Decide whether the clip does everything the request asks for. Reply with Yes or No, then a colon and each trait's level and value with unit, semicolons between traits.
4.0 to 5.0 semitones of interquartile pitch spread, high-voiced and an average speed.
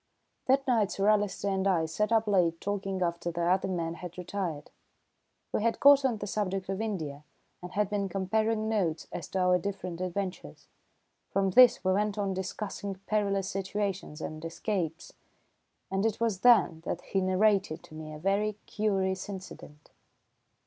No: average, 2.7 semitones; high, 195 Hz; average, 170 wpm